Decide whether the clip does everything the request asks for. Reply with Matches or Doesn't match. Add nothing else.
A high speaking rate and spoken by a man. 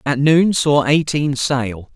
Doesn't match